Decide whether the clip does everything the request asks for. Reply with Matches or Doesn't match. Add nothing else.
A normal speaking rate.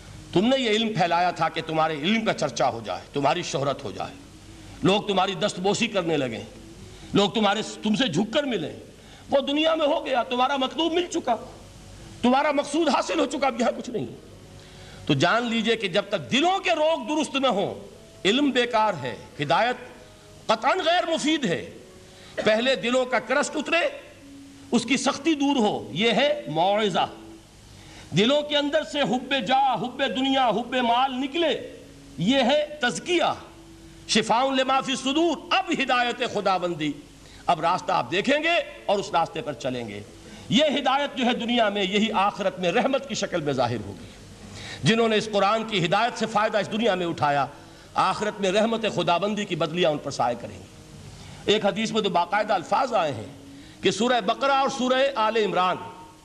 Matches